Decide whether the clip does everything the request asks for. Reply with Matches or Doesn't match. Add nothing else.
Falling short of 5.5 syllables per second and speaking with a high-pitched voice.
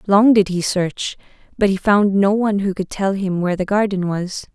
Matches